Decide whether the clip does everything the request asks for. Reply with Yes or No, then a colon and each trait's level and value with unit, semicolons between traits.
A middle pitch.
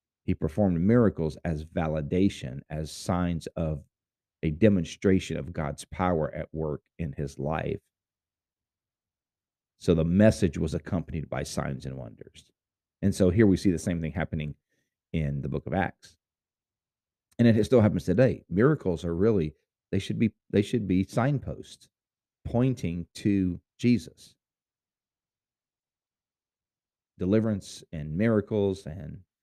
No: very low, 90 Hz